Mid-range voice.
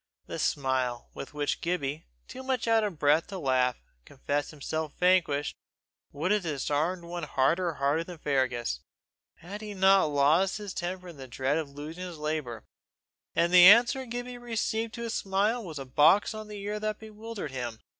Yes: medium, 170 Hz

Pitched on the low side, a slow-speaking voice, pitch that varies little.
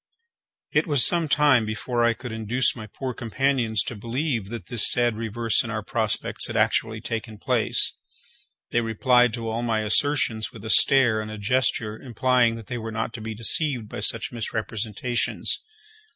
No: low, 115 Hz; average, 175 wpm; narrow, 2.3 semitones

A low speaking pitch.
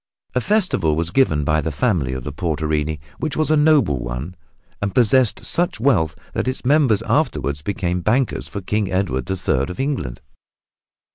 Yes: very low, 95 Hz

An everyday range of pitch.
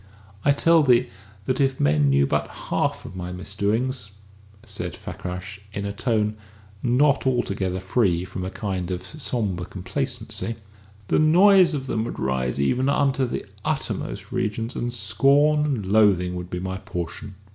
No: wide, 6.2 semitones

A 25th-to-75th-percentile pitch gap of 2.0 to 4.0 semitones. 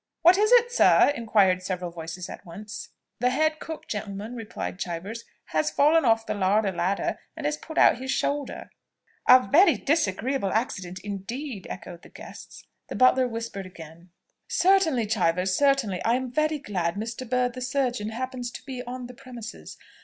No: wide, 5.5 semitones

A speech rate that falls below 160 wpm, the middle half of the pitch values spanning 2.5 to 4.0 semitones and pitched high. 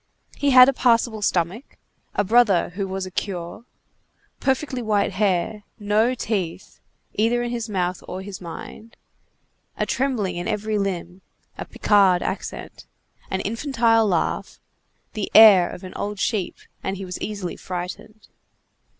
Yes: average, 140 wpm; average, 3.4 semitones; high, 205 Hz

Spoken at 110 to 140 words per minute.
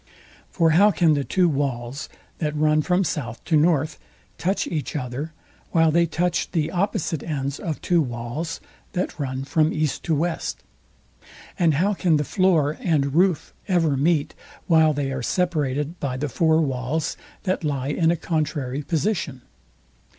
No: average, 160 wpm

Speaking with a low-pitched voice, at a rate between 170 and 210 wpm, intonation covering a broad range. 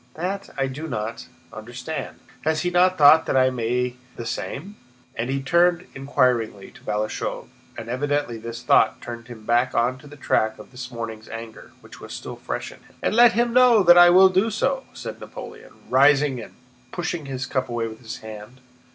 Yes: low, 130 Hz; average, 195 wpm; wide, 6.6 semitones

